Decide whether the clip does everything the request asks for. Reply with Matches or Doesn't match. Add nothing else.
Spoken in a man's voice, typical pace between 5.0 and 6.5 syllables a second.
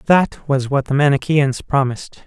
Doesn't match